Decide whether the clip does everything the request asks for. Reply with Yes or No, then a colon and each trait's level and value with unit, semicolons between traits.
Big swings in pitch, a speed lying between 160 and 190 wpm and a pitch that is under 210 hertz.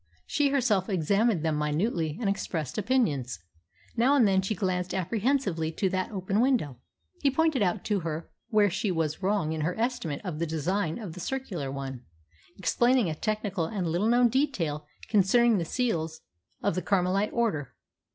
Yes: wide, 6.0 semitones; average, 170 wpm; high, 190 Hz